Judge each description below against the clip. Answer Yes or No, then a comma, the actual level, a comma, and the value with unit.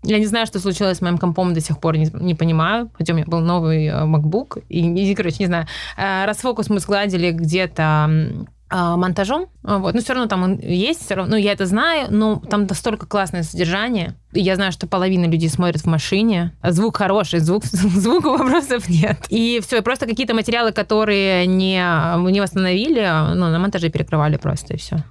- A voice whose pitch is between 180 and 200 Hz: Yes, high, 190 Hz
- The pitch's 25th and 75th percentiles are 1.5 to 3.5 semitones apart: No, average, 4.0 semitones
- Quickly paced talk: Yes, fast, 195 wpm